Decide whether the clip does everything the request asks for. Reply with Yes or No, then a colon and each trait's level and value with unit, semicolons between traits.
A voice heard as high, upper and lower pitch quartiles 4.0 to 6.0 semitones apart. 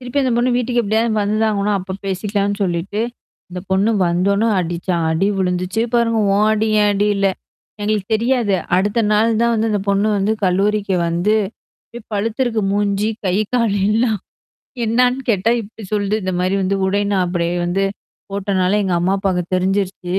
No: high, 200 Hz; average, 2.7 semitones